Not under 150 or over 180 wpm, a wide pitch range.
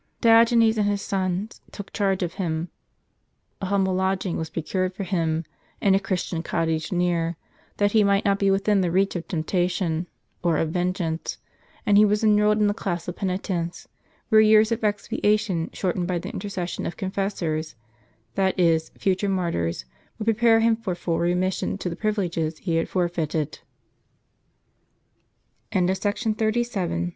No: average, 155 wpm; average, 3.2 semitones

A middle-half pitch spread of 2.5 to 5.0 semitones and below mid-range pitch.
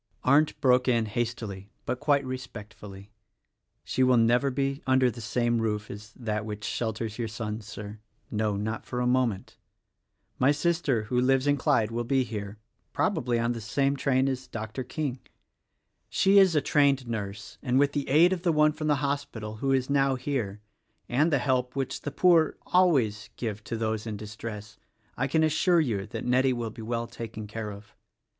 Yes: average, 4.0 semitones; low, 125 Hz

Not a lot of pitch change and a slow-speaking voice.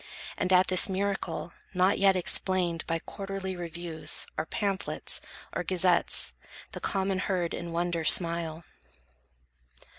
Yes: narrow, 2.0 semitones; slow, 120 wpm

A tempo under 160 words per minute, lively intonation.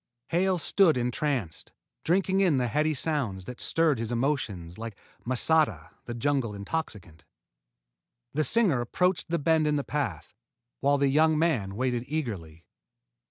Yes: average, 140 wpm; wide, 6.1 semitones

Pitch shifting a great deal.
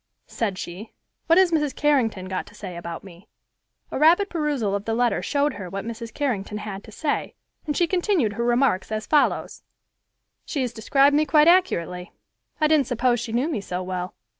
Yes: wide, 7.1 semitones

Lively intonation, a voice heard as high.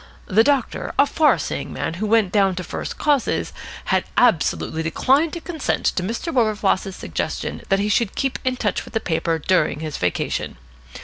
Yes: wide, 6.2 semitones; high, 210 Hz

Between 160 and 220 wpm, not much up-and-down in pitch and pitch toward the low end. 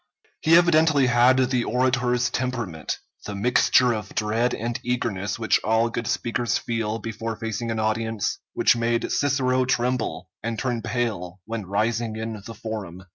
No: average, 150 wpm; narrow, 2.2 semitones; low, 115 Hz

